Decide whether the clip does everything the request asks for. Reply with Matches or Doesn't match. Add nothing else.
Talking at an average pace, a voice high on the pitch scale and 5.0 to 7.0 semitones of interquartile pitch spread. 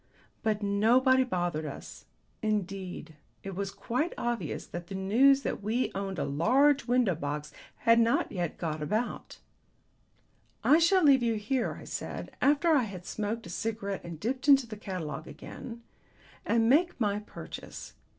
Matches